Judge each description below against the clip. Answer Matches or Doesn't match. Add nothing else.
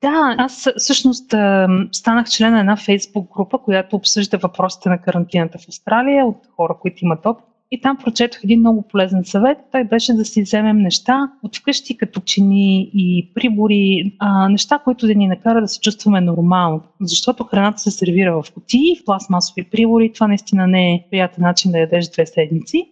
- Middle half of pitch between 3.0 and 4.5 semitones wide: Matches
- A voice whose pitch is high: Matches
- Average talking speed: Doesn't match